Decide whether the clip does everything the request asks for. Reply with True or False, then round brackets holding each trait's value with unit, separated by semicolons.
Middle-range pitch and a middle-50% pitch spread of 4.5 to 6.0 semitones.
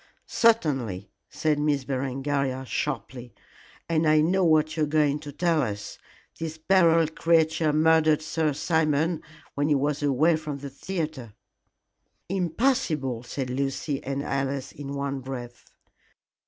False (150 Hz; 2.9 semitones)